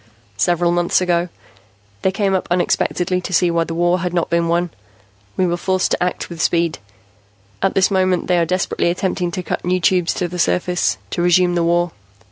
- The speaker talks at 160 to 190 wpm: No, average, 200 wpm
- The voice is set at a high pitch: No, medium, 175 Hz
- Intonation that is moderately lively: No, narrow, 1.1 semitones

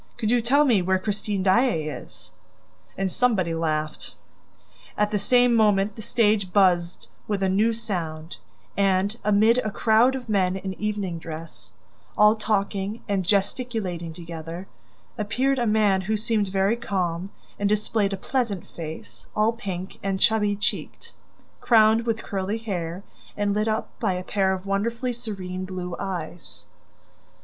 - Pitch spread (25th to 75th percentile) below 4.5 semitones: Yes, average, 3.0 semitones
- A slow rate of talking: No, average, 150 wpm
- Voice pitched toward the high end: Yes, high, 200 Hz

